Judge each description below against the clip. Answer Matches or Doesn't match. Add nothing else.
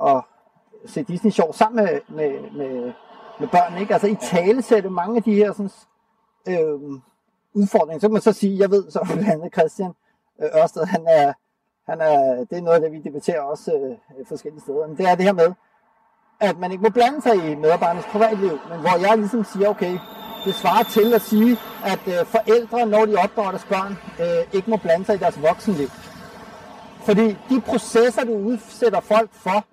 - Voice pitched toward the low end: Doesn't match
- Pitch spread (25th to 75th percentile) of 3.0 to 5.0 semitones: Matches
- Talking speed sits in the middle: Matches